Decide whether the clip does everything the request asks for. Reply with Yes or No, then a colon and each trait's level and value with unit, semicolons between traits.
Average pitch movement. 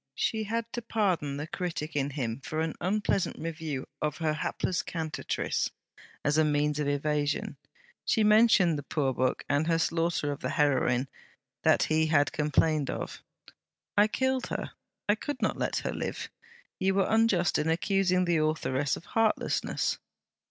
Yes: average, 4.7 semitones